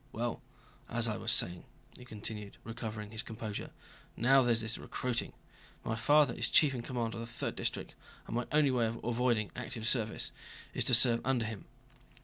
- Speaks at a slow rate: No, average, 180 wpm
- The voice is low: Yes, low, 115 Hz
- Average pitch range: No, narrow, 2.0 semitones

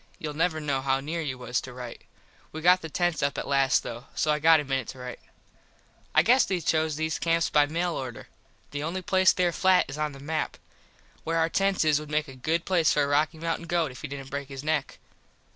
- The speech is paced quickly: Yes, fast, 240 wpm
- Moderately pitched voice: Yes, medium, 155 Hz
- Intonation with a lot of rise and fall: No, average, 3.2 semitones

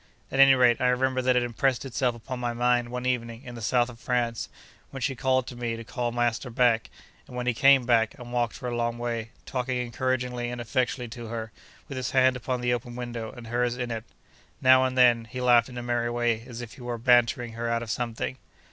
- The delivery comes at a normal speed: No, fast, 235 wpm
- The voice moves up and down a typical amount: No, narrow, 1.2 semitones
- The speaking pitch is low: Yes, low, 120 Hz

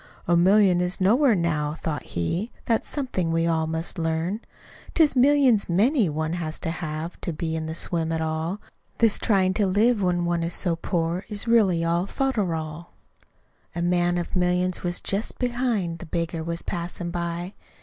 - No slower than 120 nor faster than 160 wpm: No, average, 175 wpm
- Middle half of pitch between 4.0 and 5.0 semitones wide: No, average, 3.5 semitones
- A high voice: No, medium, 175 Hz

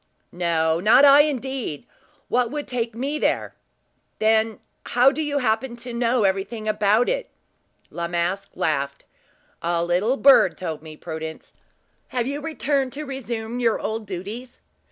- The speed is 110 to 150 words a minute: Yes, average, 145 wpm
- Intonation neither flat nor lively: No, wide, 6.6 semitones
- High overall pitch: Yes, high, 225 Hz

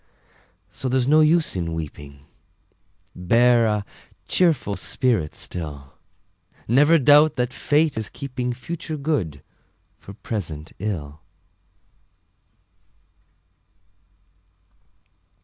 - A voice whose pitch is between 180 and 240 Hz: No, low, 120 Hz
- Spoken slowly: Yes, slow, 85 wpm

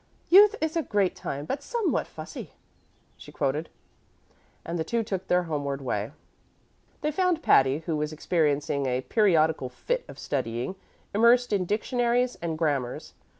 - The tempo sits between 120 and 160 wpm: Yes, average, 150 wpm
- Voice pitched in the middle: Yes, medium, 170 Hz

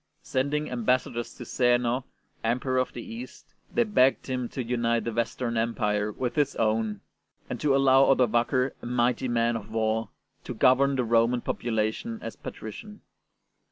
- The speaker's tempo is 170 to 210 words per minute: No, average, 160 wpm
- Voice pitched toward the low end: Yes, low, 120 Hz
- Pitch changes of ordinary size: No, narrow, 2.3 semitones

